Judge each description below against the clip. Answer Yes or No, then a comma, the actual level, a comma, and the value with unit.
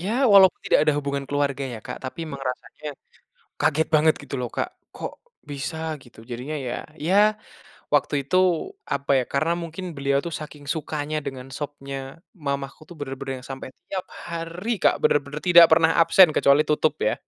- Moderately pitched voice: Yes, medium, 145 Hz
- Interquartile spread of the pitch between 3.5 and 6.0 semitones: No, average, 3.1 semitones